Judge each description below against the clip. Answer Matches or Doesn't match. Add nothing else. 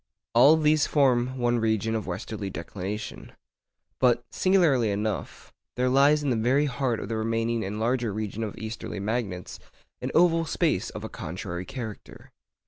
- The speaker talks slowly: Doesn't match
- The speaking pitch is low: Matches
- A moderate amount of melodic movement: Matches